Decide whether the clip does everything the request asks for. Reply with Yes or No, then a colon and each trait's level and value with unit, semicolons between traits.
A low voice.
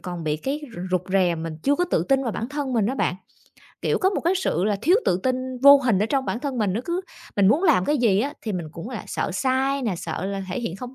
No: high, 235 Hz